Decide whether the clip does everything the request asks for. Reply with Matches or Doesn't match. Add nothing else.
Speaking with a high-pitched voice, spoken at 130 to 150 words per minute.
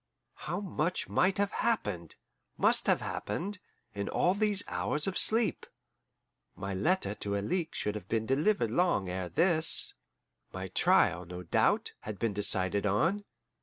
Doesn't match